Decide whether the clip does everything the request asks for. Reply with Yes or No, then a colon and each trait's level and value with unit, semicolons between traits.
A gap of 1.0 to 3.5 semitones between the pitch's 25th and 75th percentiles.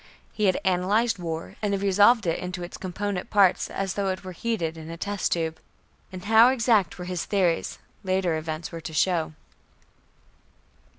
Yes: average, 3.2 semitones